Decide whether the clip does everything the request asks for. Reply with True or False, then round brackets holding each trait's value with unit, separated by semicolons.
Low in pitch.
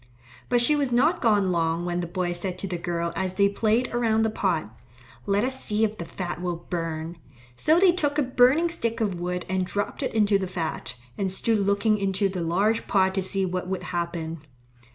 False (195 Hz)